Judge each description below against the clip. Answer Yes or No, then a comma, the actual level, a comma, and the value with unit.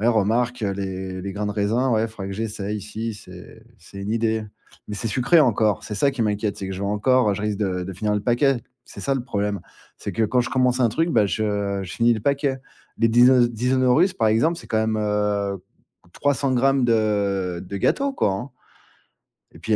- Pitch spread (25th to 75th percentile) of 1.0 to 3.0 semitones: No, average, 3.5 semitones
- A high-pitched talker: No, low, 110 Hz